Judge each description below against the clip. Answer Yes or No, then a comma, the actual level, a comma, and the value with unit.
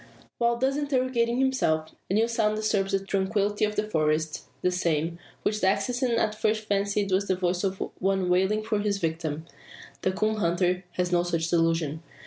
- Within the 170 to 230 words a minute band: Yes, average, 180 wpm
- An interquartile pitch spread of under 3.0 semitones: No, average, 3.6 semitones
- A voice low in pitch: No, high, 195 Hz